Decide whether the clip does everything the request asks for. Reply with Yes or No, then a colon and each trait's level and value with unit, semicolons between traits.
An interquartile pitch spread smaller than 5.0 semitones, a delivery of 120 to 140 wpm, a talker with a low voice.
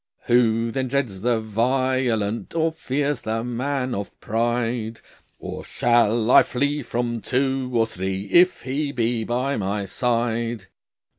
Yes: average, 2.7 semitones; slow, 135 wpm; low, 120 Hz